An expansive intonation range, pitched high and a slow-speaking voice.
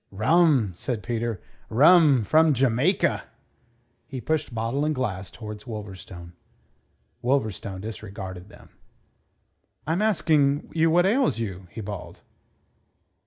No: wide, 7.1 semitones; low, 120 Hz; slow, 110 wpm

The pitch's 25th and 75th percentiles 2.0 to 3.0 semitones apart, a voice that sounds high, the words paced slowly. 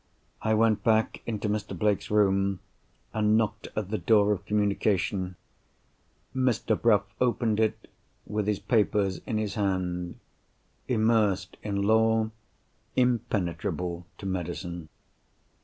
No: narrow, 2.4 semitones; low, 105 Hz; slow, 110 wpm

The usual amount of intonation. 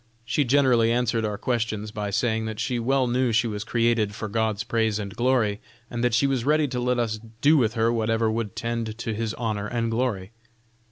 No: narrow, 2.0 semitones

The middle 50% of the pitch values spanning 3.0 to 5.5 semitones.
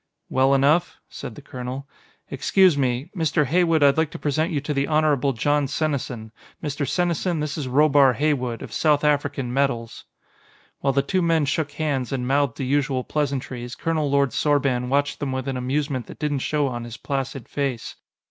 No: narrow, 2.4 semitones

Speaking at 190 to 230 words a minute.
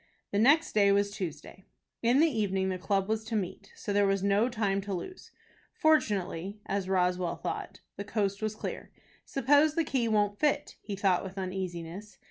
No: average, 180 wpm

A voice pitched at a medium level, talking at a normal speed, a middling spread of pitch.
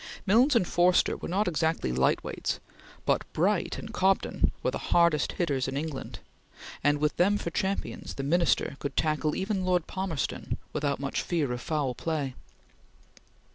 Yes: medium, 160 Hz; average, 160 wpm; average, 4.4 semitones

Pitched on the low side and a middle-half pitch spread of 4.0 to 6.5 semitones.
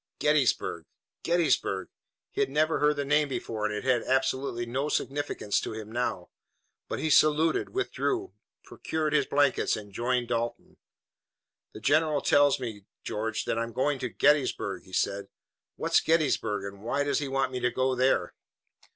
Yes: low, 130 Hz; average, 4.4 semitones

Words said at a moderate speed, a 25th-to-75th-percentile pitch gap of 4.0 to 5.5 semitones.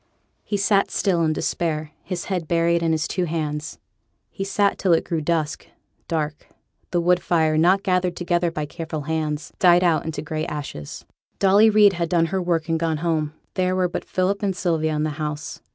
No: average, 195 wpm; narrow, 2.6 semitones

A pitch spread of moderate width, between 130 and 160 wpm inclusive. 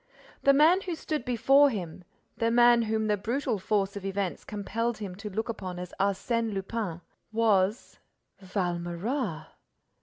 Yes: average, 3.7 semitones; average, 140 wpm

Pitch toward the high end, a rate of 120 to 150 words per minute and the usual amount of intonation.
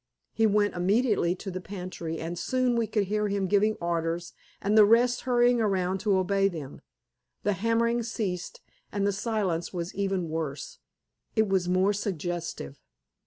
No: high, 195 Hz; average, 160 wpm; average, 3.6 semitones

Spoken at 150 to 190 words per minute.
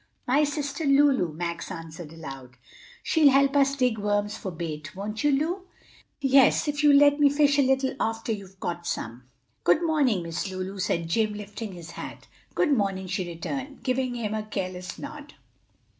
Yes: average, 175 wpm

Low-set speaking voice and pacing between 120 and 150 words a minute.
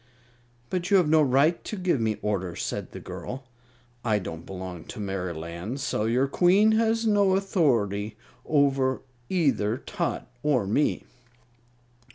Yes: low, 130 Hz; average, 140 wpm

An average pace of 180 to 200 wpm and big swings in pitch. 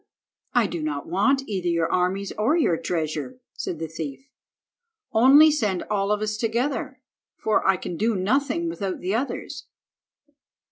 No: average, 150 wpm; wide, 6.4 semitones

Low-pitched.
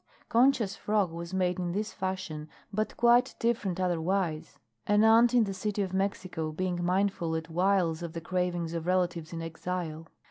No: medium, 185 Hz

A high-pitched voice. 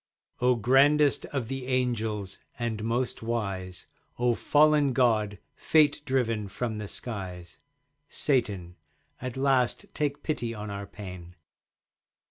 No: low, 120 Hz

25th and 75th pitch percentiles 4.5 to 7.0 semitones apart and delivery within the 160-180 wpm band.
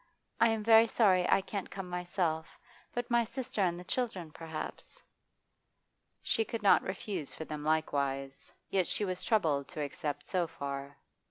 Yes: wide, 5.6 semitones; average, 165 wpm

